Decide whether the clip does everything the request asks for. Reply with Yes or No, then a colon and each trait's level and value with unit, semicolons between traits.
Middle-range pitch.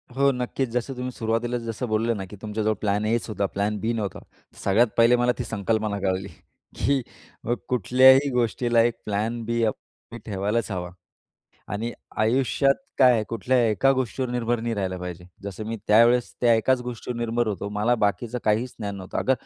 No: low, 115 Hz